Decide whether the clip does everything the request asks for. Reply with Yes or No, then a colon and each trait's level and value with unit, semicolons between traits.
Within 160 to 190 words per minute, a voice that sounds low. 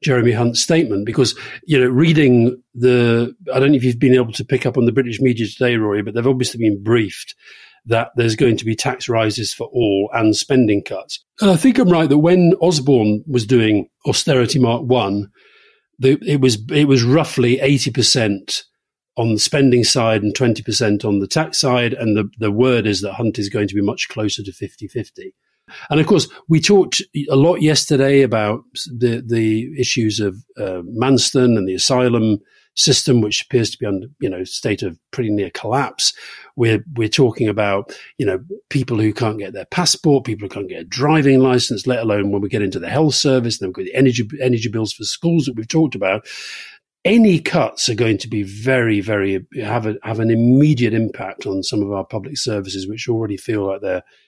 No: average, 200 wpm; low, 120 Hz